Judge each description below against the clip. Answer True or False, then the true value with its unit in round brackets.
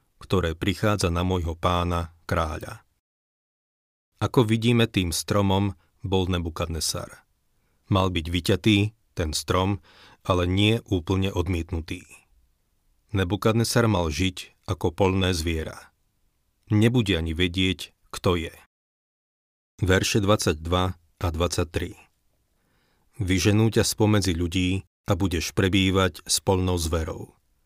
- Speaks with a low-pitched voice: True (95 Hz)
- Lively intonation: False (2.9 semitones)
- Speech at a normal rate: False (100 wpm)